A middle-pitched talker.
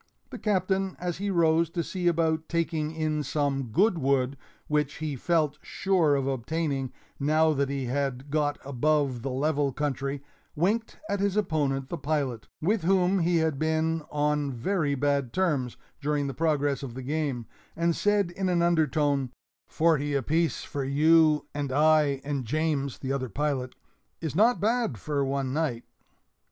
Yes: medium, 150 Hz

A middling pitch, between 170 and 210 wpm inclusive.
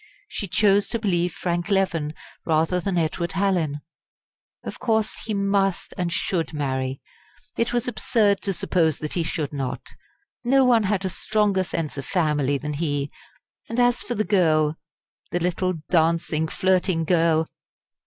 No: medium, 175 Hz; average, 155 wpm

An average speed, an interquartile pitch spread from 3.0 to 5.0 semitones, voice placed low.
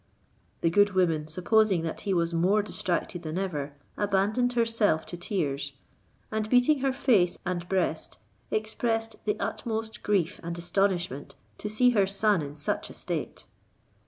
No: average, 150 wpm; average, 4.2 semitones; high, 195 Hz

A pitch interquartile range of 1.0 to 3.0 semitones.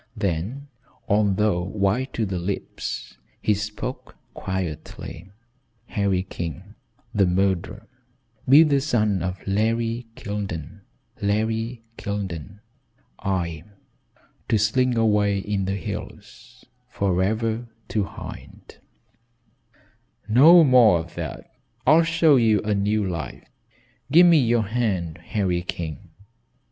No: average, 3.6 semitones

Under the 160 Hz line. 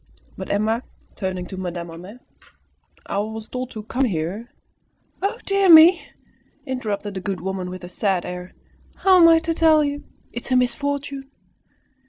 No: high, 220 Hz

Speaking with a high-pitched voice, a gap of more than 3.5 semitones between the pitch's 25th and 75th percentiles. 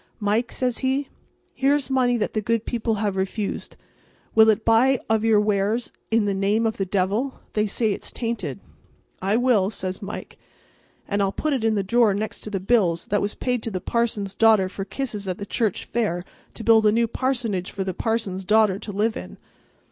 No: high, 215 Hz; average, 2.8 semitones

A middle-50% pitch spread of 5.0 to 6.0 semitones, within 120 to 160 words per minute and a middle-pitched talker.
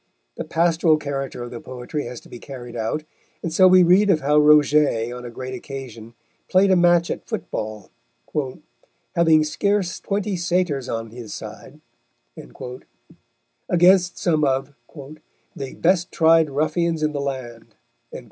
Yes: wide, 5.4 semitones; average, 145 wpm; medium, 150 Hz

